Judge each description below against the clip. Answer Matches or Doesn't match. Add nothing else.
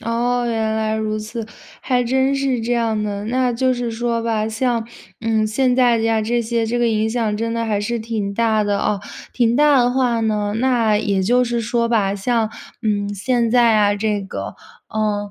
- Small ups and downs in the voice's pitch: Matches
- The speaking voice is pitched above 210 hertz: Matches